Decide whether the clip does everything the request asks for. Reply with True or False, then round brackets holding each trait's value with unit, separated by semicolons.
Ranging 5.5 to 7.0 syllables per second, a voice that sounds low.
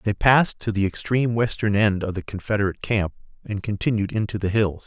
True (6.1 syllables/s; 105 Hz)